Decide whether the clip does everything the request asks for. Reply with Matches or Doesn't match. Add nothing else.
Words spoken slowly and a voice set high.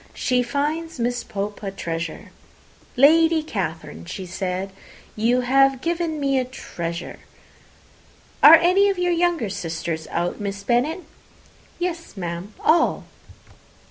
Matches